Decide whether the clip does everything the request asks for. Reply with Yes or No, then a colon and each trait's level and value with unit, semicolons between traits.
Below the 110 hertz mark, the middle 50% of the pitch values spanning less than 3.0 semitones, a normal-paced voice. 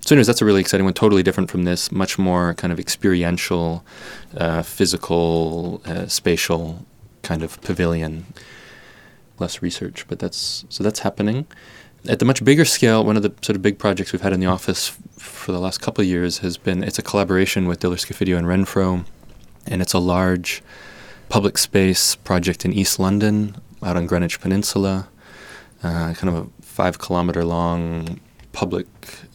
Yes: very low, 95 Hz; narrow, 2.6 semitones; average, 175 wpm